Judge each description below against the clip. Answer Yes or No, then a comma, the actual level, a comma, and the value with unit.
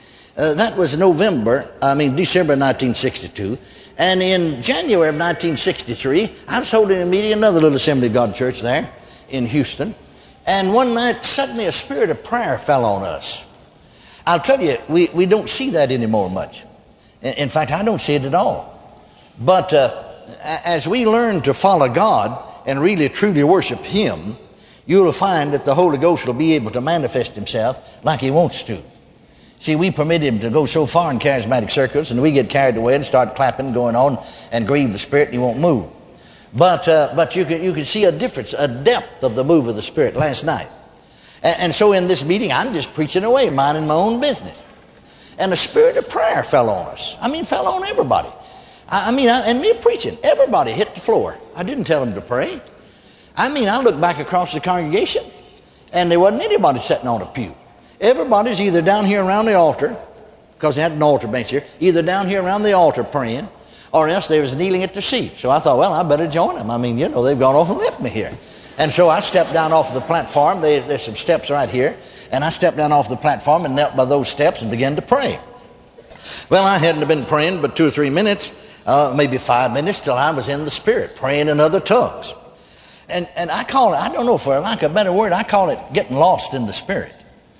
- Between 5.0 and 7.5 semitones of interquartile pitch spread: Yes, wide, 5.6 semitones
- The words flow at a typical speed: No, fast, 215 wpm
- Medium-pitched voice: Yes, medium, 165 Hz